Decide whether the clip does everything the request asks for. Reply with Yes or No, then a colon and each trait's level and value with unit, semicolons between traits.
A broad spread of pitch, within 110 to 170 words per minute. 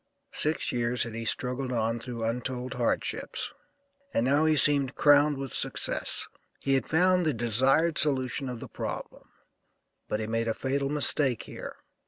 No: average, 3.5 semitones; average, 160 wpm